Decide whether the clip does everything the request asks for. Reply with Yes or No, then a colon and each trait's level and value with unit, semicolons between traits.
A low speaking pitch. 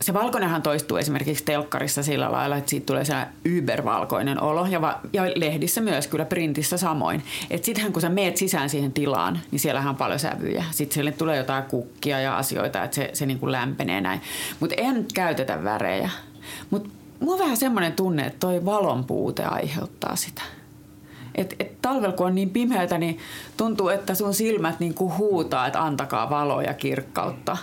No: medium, 165 Hz